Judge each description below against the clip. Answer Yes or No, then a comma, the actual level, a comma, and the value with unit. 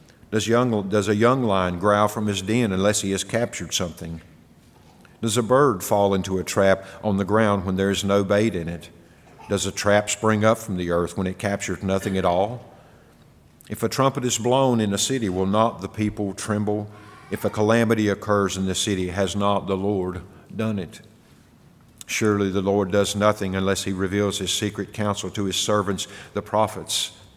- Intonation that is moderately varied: No, narrow, 1.9 semitones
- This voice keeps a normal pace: Yes, average, 195 wpm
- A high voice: No, low, 100 Hz